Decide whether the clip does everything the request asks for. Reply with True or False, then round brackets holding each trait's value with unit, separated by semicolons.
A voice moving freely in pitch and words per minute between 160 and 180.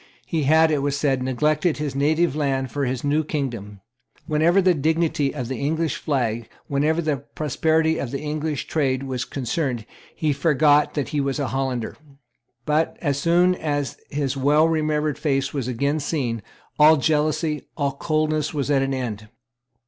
False (2.4 semitones; 165 wpm)